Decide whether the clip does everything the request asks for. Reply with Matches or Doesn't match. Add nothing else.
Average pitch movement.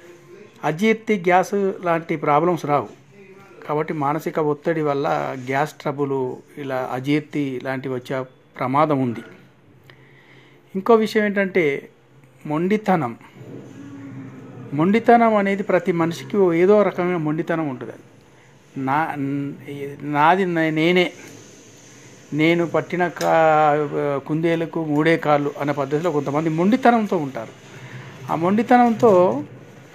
Matches